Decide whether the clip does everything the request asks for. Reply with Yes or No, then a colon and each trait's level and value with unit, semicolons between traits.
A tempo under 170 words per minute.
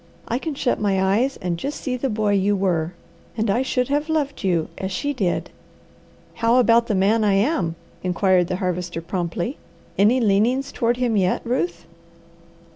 No: average, 175 wpm